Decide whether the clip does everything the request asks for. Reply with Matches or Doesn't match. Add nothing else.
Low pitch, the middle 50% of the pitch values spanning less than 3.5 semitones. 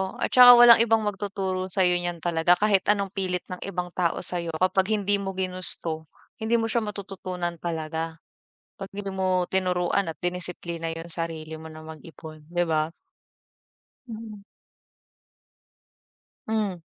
Doesn't match